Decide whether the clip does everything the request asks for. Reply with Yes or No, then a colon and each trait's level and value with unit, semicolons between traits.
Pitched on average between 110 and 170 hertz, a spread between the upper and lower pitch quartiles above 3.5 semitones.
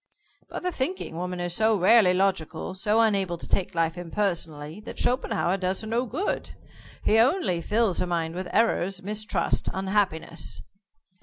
No: high, 190 Hz; average, 4.0 semitones